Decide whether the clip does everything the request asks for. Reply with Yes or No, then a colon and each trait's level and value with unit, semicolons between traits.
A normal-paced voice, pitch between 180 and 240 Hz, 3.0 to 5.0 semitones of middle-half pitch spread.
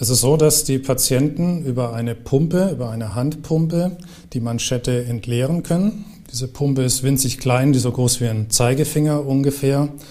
No: average, 170 wpm; low, 135 Hz; average, 3.6 semitones